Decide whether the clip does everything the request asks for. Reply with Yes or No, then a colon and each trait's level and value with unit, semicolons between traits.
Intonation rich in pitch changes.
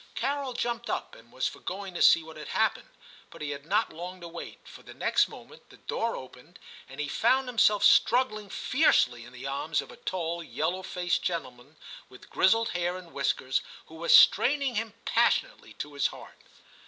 Yes: wide, 7.6 semitones